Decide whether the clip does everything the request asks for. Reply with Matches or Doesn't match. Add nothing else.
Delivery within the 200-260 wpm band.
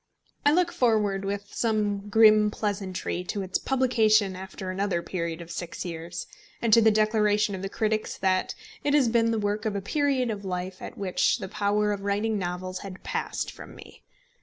Doesn't match